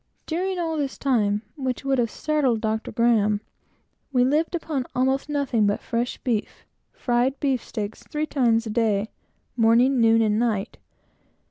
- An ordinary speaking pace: Yes, average, 145 wpm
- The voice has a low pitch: No, high, 245 Hz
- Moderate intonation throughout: Yes, average, 3.7 semitones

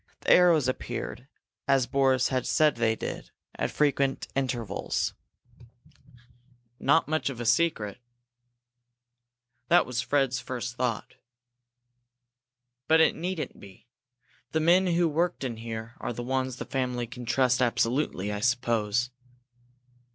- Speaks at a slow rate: Yes, slow, 125 wpm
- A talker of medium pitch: No, low, 130 Hz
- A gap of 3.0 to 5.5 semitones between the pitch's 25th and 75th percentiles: Yes, average, 3.6 semitones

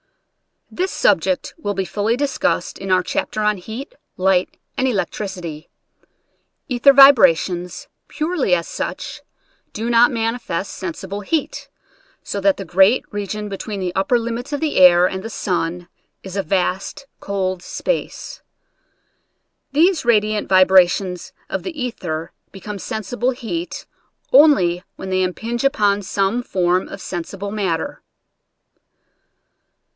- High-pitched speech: Yes, high, 200 Hz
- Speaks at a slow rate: Yes, slow, 130 wpm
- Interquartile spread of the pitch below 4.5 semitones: No, average, 4.8 semitones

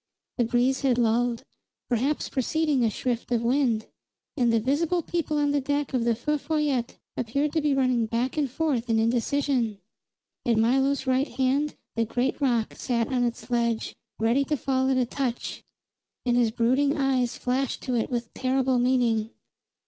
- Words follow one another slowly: No, average, 170 wpm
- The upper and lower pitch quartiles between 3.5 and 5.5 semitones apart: No, average, 3.0 semitones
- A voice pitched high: Yes, very high, 255 Hz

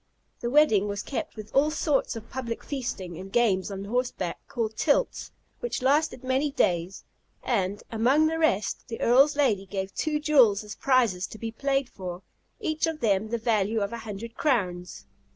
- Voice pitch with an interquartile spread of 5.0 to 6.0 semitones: Yes, wide, 5.5 semitones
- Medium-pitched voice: No, high, 230 Hz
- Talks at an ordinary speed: Yes, average, 175 wpm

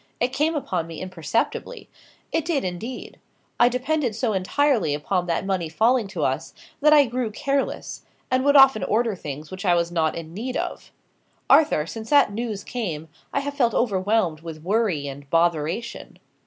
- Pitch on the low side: No, high, 210 Hz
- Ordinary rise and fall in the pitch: No, wide, 7.3 semitones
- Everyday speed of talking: Yes, average, 170 wpm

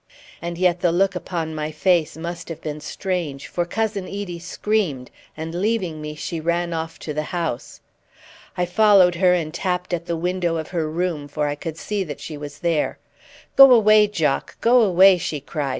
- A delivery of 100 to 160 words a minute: No, average, 190 wpm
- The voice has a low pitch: No, medium, 170 Hz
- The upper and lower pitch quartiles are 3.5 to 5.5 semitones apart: No, average, 3.1 semitones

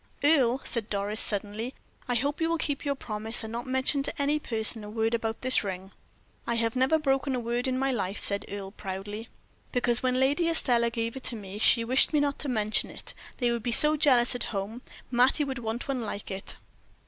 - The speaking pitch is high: Yes, high, 240 Hz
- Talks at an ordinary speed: No, fast, 220 wpm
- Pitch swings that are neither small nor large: Yes, average, 3.5 semitones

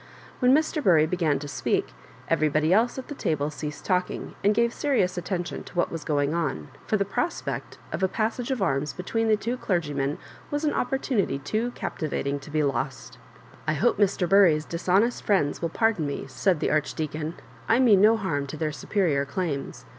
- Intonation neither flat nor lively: No, wide, 6.5 semitones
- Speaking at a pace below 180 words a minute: No, average, 195 wpm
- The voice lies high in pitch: No, medium, 175 Hz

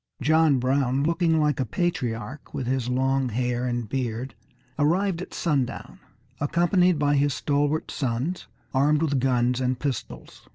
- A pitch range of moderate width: Yes, average, 3.7 semitones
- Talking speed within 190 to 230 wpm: No, average, 140 wpm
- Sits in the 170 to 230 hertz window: No, low, 135 Hz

